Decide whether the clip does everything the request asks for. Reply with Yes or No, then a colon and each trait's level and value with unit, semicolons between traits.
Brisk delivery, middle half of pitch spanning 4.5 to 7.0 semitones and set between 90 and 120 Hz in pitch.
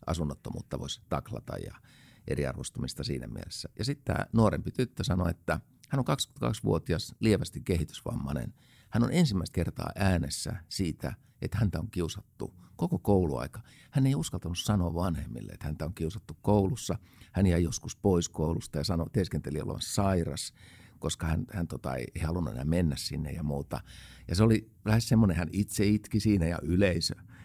Yes: fast, 160 wpm; average, 4.9 semitones; very low, 95 Hz